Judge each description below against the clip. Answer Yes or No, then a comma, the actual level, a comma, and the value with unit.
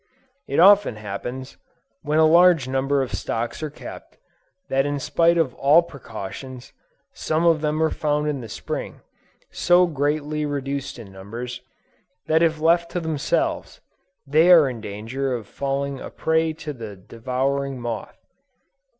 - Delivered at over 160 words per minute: No, average, 150 wpm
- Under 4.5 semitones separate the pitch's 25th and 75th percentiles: Yes, average, 4.0 semitones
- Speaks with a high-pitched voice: No, medium, 140 Hz